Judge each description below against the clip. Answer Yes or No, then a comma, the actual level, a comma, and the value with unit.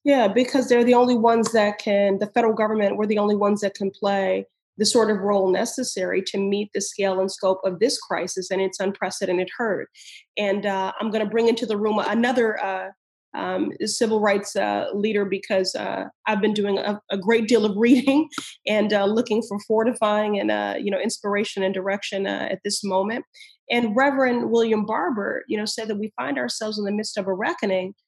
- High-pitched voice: Yes, high, 210 Hz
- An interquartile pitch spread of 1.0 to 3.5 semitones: Yes, narrow, 2.6 semitones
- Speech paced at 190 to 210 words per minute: Yes, fast, 205 wpm